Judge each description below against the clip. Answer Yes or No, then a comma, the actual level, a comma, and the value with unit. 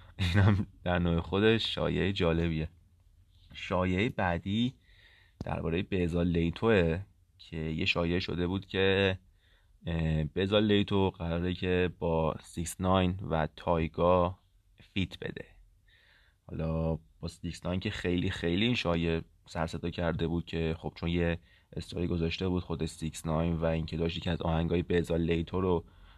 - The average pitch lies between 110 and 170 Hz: No, very low, 85 Hz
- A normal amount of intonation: No, narrow, 2.1 semitones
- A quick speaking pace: No, average, 130 wpm